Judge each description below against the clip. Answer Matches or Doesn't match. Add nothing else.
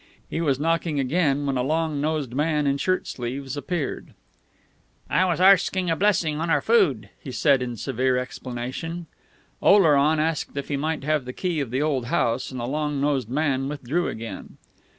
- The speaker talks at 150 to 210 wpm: Matches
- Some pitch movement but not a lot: Matches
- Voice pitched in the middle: Matches